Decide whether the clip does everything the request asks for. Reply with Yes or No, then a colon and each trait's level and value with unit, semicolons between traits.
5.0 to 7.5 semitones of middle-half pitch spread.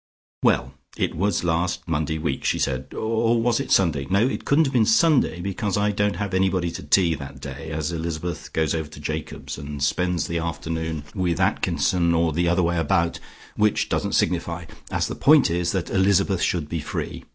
No: average, 3.8 semitones